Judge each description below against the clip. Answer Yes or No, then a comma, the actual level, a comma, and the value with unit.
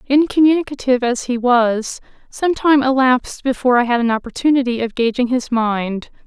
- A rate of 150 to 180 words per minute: Yes, average, 155 wpm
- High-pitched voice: Yes, very high, 250 Hz